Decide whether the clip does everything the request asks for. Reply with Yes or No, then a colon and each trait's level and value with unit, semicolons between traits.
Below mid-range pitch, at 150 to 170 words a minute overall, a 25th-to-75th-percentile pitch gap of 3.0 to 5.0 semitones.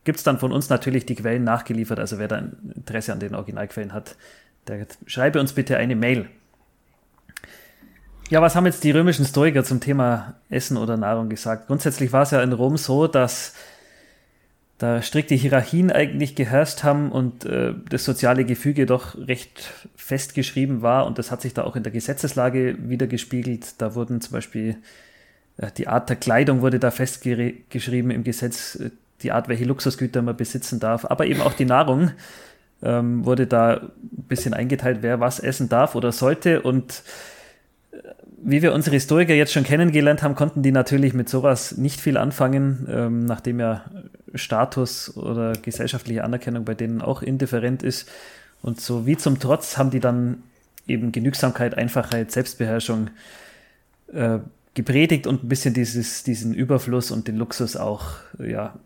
No: low, 125 Hz; average, 165 wpm; narrow, 2.6 semitones